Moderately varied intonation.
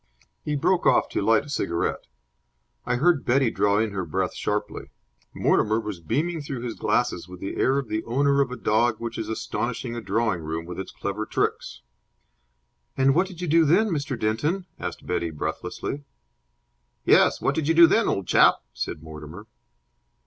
No: wide, 6.3 semitones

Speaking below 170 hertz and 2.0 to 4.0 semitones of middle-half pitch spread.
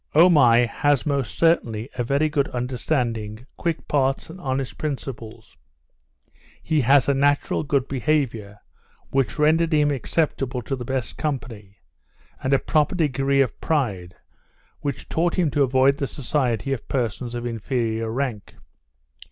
Yes: low, 135 Hz; average, 3.5 semitones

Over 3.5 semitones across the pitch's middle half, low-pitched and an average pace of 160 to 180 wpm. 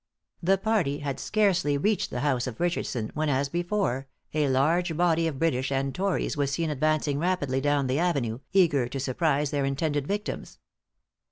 No: average, 4.2 semitones; medium, 145 Hz; average, 170 wpm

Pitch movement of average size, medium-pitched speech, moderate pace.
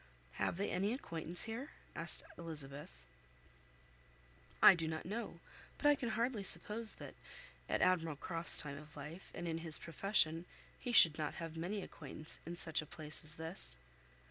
Yes: average, 4.2 semitones; medium, 165 Hz; average, 165 wpm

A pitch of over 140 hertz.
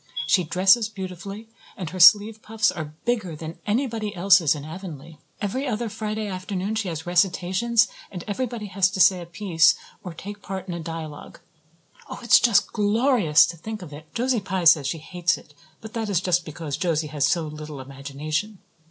Yes: medium, 185 Hz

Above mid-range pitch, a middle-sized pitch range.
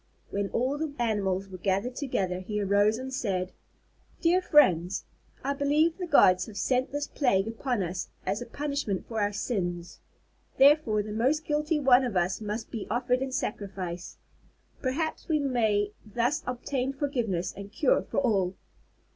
No: high, 230 Hz; wide, 5.8 semitones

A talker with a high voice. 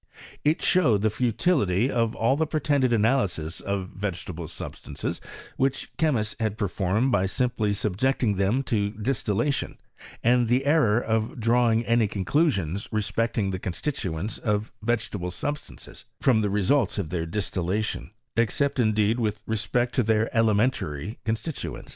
No: low, 110 Hz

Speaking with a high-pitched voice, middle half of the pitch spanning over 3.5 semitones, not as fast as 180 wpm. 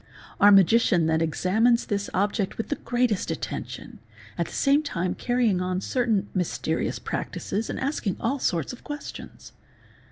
Yes: high, 205 Hz; average, 5.0 semitones; average, 155 wpm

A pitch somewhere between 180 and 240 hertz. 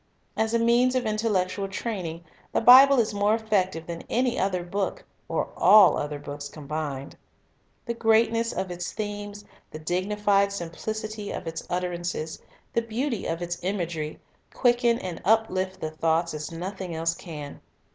Yes: high, 190 Hz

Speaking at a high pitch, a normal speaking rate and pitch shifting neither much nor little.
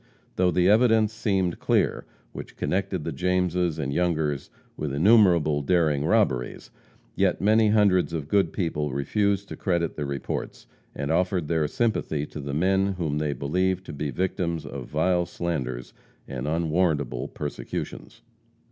No: very low, 85 Hz; average, 145 wpm; average, 4.1 semitones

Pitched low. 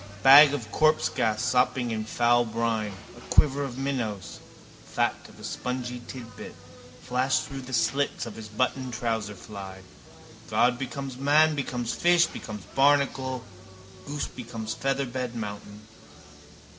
Yes: low, 125 Hz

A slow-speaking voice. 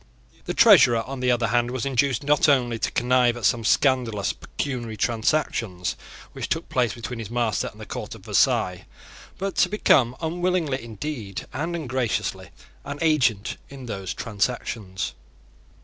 No: average, 150 wpm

